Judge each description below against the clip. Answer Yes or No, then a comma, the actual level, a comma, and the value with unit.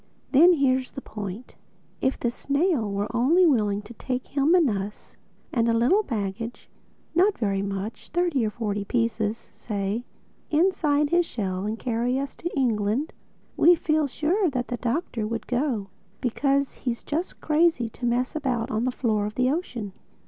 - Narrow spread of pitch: No, wide, 5.5 semitones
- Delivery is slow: No, average, 155 wpm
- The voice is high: Yes, high, 245 Hz